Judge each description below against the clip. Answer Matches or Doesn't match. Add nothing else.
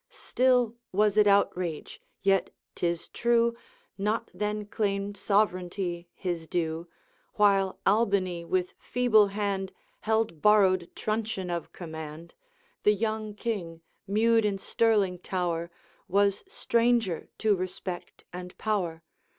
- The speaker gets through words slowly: Matches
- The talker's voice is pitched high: Matches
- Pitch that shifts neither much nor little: Matches